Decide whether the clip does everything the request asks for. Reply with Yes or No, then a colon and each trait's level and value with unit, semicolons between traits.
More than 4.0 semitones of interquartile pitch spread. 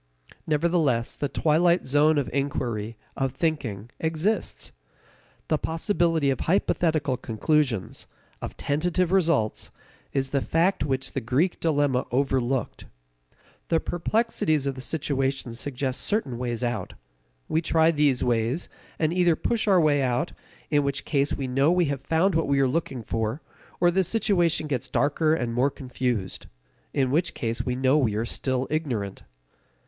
Yes: average, 4.4 semitones